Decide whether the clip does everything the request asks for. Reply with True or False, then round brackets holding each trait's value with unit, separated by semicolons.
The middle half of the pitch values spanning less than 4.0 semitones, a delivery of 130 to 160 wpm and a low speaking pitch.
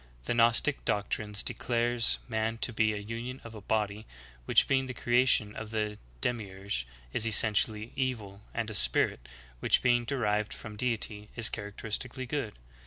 True (2.5 semitones; 155 wpm; 110 Hz)